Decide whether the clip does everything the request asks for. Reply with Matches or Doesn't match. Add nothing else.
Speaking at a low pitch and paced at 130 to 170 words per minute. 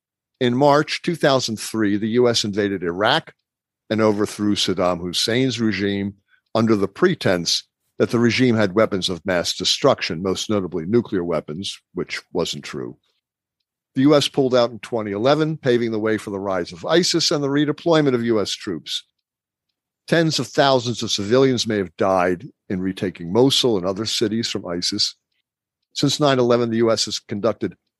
Matches